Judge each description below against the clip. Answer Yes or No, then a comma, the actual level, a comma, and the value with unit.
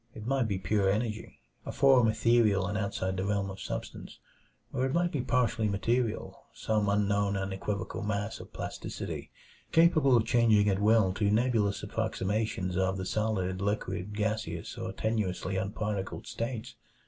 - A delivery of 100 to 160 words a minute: Yes, average, 155 wpm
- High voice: No, low, 105 Hz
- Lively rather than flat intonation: No, average, 2.7 semitones